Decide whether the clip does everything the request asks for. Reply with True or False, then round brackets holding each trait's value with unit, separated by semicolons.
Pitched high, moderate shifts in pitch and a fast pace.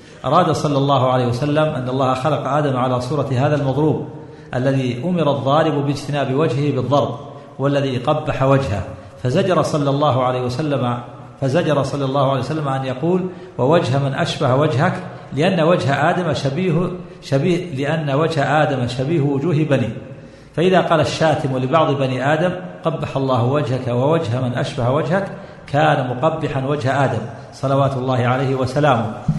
False (140 Hz; 3.0 semitones; 145 wpm)